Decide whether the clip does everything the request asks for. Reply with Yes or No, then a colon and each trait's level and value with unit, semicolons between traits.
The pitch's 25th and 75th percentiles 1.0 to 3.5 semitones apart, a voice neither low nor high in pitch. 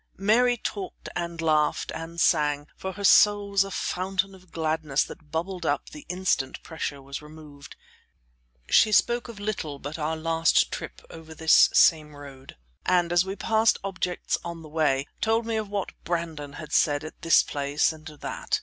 No: average, 4.3 semitones; medium, 165 Hz